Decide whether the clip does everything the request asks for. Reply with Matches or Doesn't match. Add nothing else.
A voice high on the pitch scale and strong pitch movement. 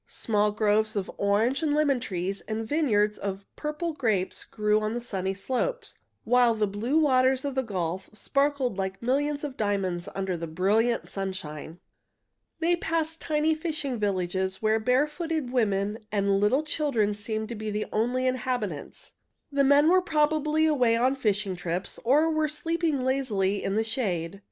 Matches